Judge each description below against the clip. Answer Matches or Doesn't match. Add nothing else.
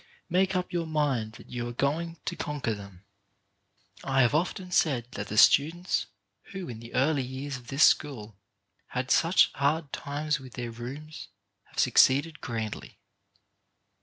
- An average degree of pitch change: Matches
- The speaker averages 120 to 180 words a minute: Matches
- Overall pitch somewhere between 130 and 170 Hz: Matches